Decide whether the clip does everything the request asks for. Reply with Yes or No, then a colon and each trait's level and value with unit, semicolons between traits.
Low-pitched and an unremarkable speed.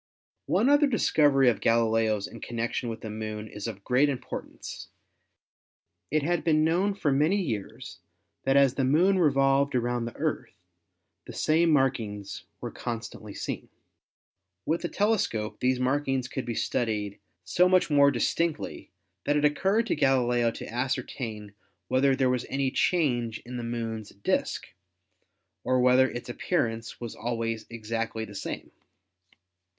Yes: low, 125 Hz; average, 150 wpm